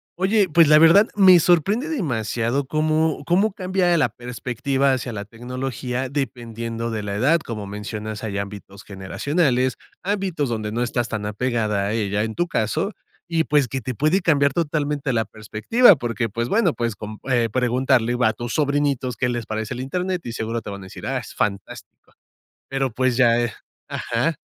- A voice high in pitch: No, low, 125 Hz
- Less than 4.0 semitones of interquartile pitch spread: No, wide, 5.5 semitones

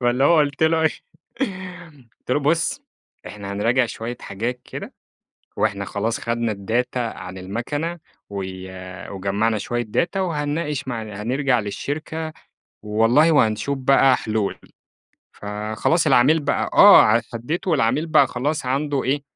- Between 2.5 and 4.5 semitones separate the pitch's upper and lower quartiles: No, average, 5.3 semitones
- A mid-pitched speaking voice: No, low, 125 Hz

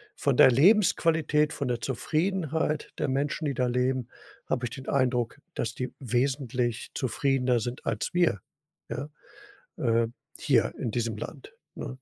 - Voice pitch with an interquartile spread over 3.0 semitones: Yes, average, 3.7 semitones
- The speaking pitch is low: Yes, low, 130 Hz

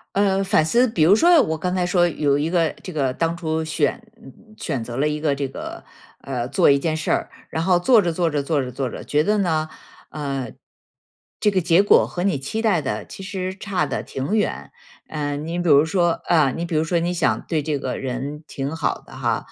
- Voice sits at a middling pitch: Yes, medium, 160 Hz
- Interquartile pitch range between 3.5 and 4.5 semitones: Yes, average, 4.1 semitones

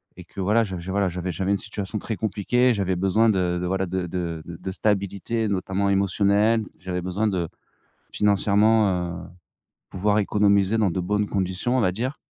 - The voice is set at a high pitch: No, low, 100 Hz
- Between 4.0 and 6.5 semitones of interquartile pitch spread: No, narrow, 2.5 semitones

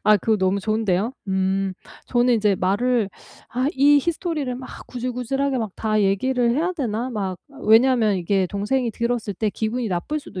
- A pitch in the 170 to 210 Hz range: No, high, 225 Hz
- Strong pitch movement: No, average, 4.2 semitones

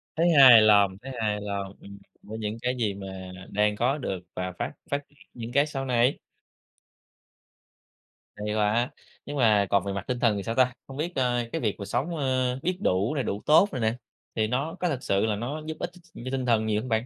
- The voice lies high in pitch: No, low, 120 Hz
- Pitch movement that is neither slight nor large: Yes, average, 4.4 semitones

